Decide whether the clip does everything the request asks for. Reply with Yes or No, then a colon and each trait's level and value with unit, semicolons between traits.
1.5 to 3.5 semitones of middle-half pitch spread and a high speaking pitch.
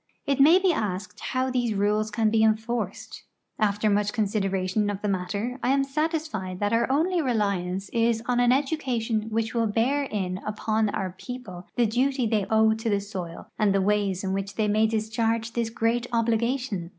Yes: average, 3.1 semitones; high, 220 Hz